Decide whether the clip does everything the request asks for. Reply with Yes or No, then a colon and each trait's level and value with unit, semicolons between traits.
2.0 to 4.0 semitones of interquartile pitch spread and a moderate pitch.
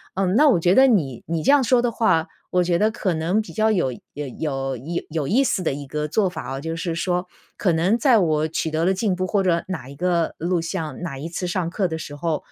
Yes: average, 3.6 semitones; medium, 175 Hz